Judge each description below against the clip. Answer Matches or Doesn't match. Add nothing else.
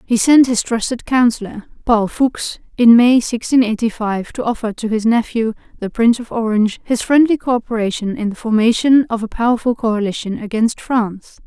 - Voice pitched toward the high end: Matches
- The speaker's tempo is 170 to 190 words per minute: Matches